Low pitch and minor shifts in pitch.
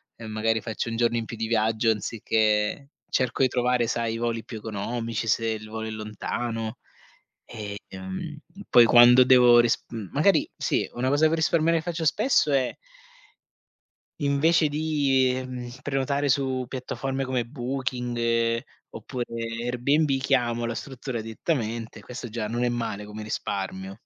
No: low, 120 Hz; average, 3.0 semitones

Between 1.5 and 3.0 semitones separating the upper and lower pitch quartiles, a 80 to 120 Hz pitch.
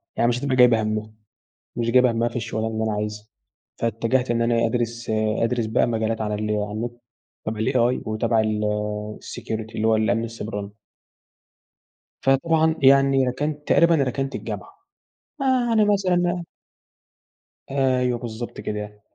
No: average, 3.4 semitones; low, 115 Hz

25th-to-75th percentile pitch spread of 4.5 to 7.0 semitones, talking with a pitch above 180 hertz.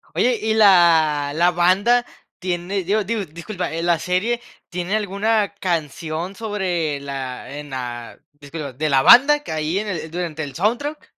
No: average, 5.1 semitones; medium, 175 Hz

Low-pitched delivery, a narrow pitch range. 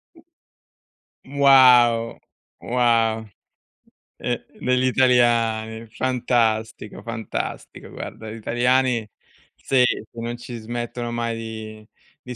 Yes: low, 120 Hz; narrow, 1.9 semitones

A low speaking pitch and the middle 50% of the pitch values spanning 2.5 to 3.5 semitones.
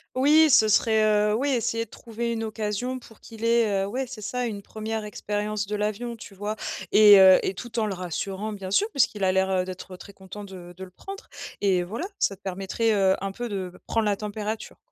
No: high, 210 Hz; average, 2.9 semitones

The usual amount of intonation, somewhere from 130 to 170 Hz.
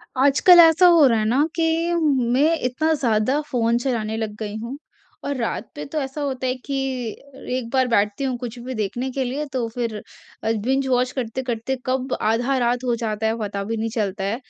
No: average, 3.3 semitones; very high, 250 Hz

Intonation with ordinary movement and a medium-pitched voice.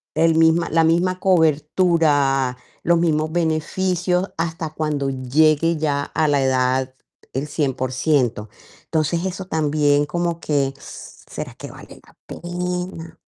Yes: average, 3.1 semitones; medium, 155 Hz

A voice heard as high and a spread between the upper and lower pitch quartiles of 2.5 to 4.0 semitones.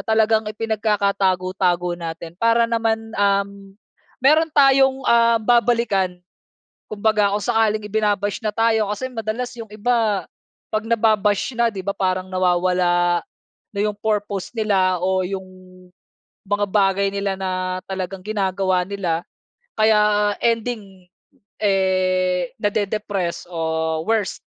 Yes: high, 205 Hz; average, 2.9 semitones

